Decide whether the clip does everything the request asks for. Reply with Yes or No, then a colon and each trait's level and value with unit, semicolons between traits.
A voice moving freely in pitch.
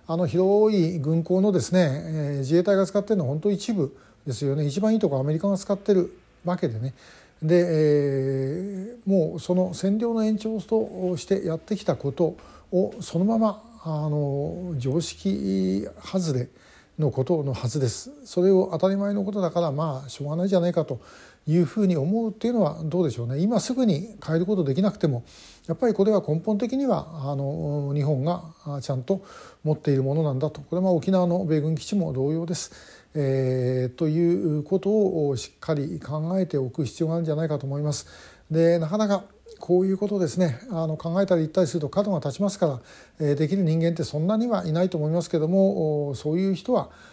No: average, 4.7 semitones